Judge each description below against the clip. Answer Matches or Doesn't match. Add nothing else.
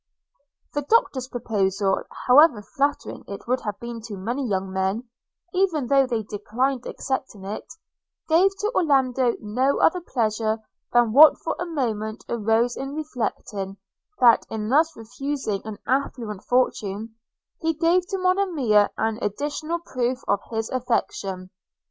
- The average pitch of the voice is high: Matches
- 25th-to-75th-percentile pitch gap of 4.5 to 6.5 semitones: Matches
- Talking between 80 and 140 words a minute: Matches